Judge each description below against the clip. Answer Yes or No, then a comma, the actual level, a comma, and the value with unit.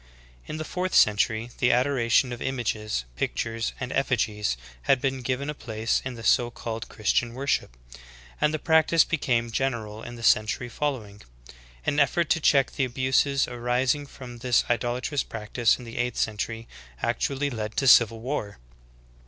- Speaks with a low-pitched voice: Yes, low, 120 Hz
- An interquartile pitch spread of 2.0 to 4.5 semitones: Yes, average, 3.3 semitones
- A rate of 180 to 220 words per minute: No, average, 170 wpm